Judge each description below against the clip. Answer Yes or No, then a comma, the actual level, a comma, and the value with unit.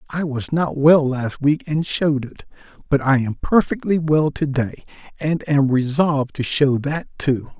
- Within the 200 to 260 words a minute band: No, average, 180 wpm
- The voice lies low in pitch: No, medium, 145 Hz